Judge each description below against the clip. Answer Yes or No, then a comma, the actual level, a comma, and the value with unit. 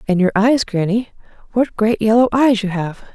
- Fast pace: No, average, 190 wpm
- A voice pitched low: No, high, 215 Hz